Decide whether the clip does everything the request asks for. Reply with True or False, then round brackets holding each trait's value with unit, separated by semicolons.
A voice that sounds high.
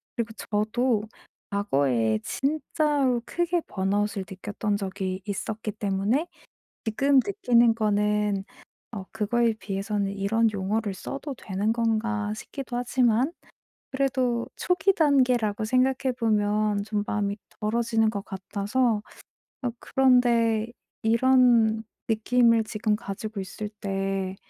True (220 Hz)